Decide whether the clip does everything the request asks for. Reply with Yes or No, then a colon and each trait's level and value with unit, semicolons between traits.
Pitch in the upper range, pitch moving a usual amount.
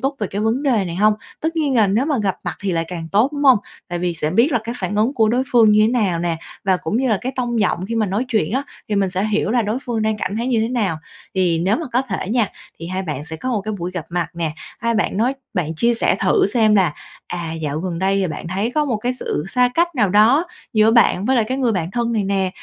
Yes: high, 215 Hz; average, 4.8 semitones